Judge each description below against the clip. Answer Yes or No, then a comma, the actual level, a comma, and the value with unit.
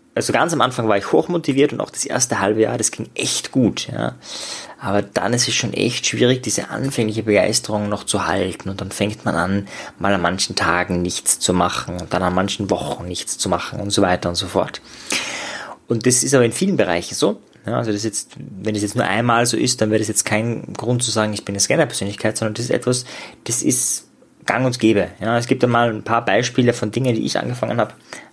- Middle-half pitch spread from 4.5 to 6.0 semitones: No, average, 2.9 semitones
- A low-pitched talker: Yes, low, 110 Hz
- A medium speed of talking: No, fast, 235 wpm